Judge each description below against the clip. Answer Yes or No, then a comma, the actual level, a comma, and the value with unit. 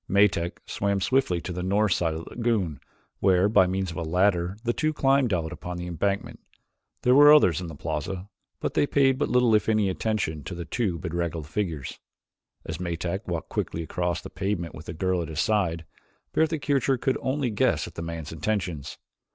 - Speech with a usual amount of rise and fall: Yes, average, 4.5 semitones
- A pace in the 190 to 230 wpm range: Yes, average, 200 wpm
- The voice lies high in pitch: No, very low, 90 Hz